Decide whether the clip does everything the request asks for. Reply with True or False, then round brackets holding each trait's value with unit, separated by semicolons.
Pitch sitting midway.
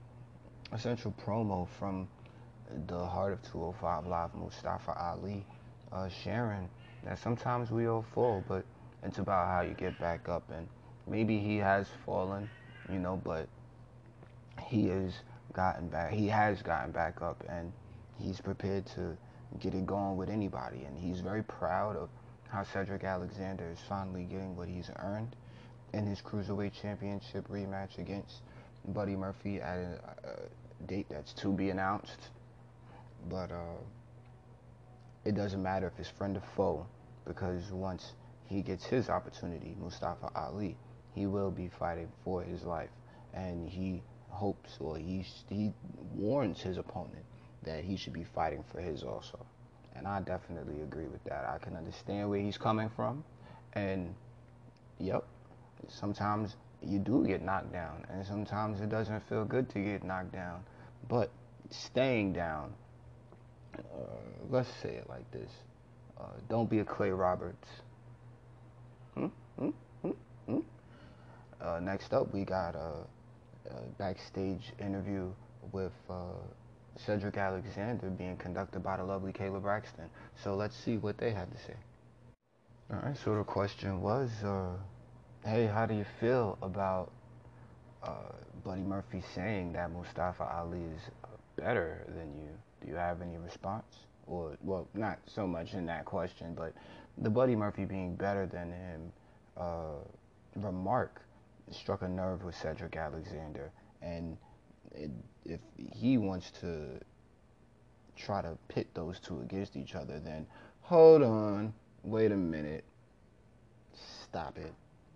False (100 Hz)